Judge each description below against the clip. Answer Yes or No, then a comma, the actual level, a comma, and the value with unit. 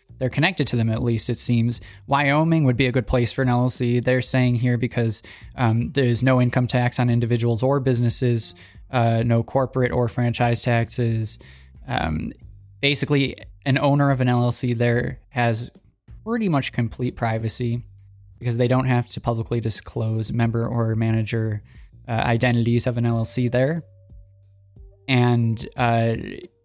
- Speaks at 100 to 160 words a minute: Yes, average, 150 wpm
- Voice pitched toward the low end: Yes, low, 120 Hz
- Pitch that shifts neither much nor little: No, narrow, 1.9 semitones